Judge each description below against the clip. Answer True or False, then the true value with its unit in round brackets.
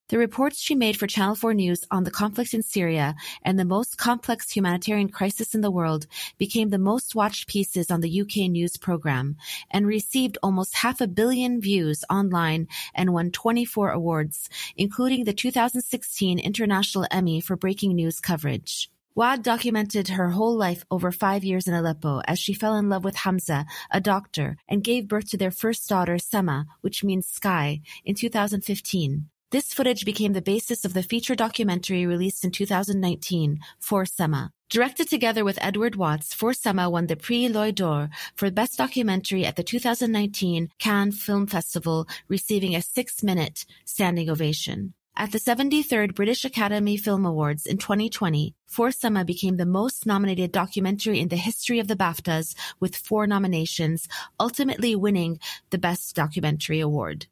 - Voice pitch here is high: True (195 Hz)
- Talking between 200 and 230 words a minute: False (160 wpm)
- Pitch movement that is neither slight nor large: True (3.8 semitones)